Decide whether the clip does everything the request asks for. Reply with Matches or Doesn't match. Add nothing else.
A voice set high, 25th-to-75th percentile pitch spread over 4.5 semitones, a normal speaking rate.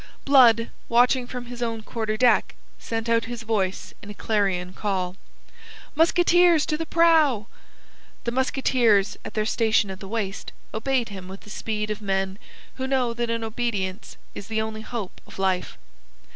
Doesn't match